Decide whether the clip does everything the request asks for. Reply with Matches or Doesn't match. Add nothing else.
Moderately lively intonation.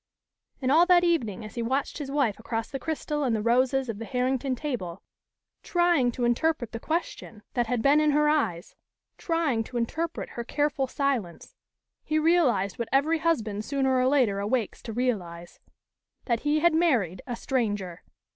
Matches